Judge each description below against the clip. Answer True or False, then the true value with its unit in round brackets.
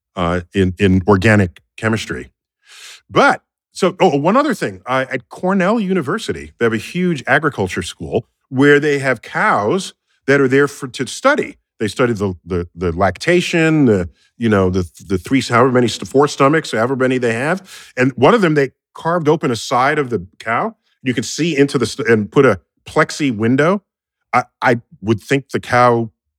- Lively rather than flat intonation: True (6.2 semitones)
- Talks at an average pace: True (180 wpm)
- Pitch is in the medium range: False (125 Hz)